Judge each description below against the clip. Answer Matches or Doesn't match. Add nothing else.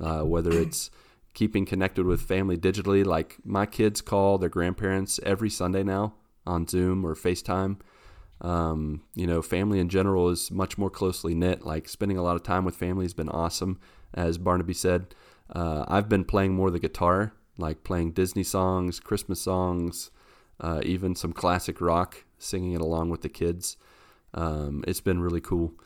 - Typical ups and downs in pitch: Doesn't match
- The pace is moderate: Matches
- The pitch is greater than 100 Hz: Doesn't match